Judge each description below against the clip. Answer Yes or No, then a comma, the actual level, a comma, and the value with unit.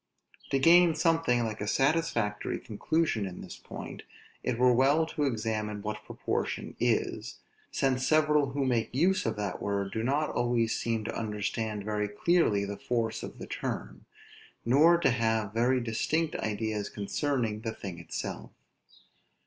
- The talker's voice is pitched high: No, low, 115 Hz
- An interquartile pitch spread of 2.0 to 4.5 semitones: No, average, 5.0 semitones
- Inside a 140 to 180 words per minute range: Yes, average, 150 wpm